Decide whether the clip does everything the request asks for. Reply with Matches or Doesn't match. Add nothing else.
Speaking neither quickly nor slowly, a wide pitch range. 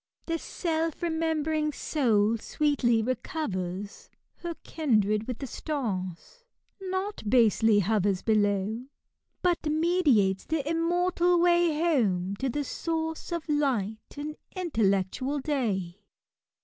Doesn't match